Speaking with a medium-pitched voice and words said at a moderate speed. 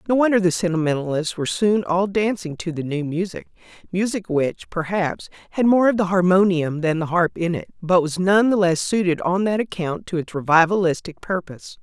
Yes: medium, 180 Hz; average, 190 wpm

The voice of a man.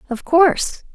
No: female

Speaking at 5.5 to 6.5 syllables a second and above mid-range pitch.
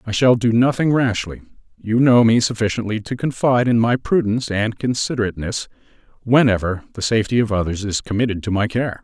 No: 6.0 syllables/s; low, 115 Hz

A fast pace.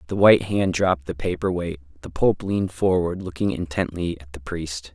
No: average, 195 wpm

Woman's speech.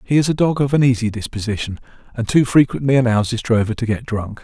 No: male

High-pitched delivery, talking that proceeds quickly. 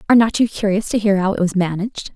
Yes: high, 200 Hz; fast, 280 wpm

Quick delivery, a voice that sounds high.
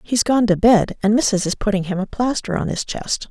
Yes: fast, 255 wpm; high, 210 Hz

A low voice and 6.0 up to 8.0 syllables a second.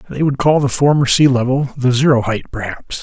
No: low, 130 Hz; 5.5 syllables/s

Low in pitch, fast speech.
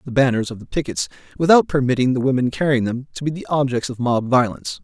Yes: low, 130 Hz; fast, 235 wpm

